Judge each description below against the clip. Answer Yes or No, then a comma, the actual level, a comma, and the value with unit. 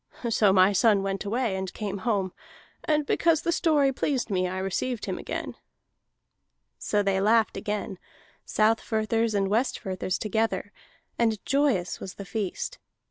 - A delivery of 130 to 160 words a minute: Yes, average, 140 wpm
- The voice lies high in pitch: Yes, high, 210 Hz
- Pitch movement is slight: No, average, 3.3 semitones